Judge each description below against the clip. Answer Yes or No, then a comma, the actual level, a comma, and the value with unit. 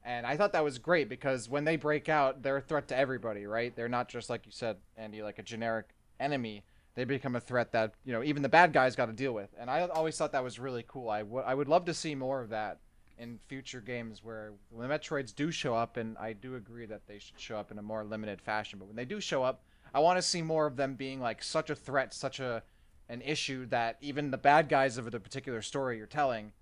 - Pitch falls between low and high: No, low, 125 Hz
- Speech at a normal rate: No, fast, 265 wpm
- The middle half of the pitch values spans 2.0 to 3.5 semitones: No, average, 3.9 semitones